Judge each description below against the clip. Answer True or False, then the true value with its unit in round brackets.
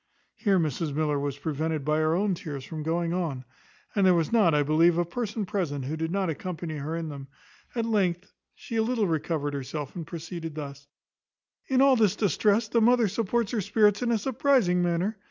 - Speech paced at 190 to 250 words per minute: True (200 wpm)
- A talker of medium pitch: True (170 Hz)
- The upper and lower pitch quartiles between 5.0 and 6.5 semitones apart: True (5.3 semitones)